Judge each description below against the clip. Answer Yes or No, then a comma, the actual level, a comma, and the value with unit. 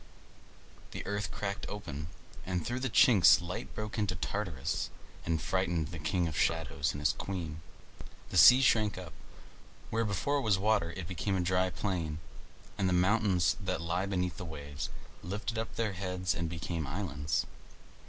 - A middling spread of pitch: Yes, average, 3.8 semitones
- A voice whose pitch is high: No, very low, 90 Hz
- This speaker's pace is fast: No, average, 165 wpm